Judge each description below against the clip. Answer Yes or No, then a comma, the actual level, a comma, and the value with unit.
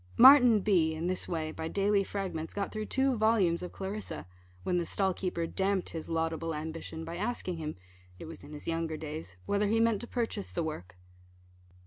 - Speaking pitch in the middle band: Yes, medium, 180 Hz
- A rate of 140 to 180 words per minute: No, average, 190 wpm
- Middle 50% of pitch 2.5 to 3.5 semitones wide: No, average, 4.3 semitones